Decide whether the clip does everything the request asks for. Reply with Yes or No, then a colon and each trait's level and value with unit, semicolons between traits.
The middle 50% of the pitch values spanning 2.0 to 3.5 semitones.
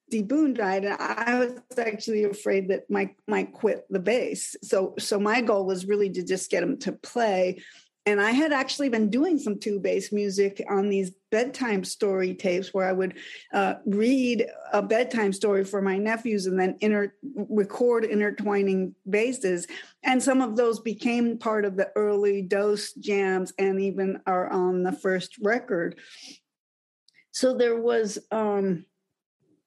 Yes: average, 3.0 semitones